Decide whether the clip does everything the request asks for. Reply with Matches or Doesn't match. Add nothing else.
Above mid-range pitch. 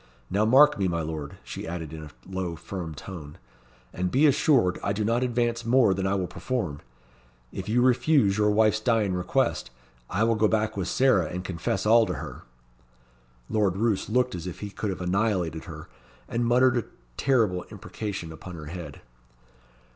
Doesn't match